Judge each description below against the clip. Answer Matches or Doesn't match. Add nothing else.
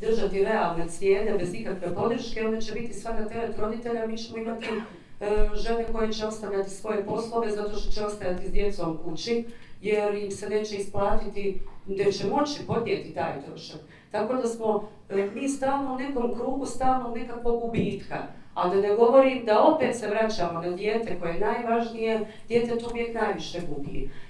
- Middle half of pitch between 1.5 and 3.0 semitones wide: Matches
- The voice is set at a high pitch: Matches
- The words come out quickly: Matches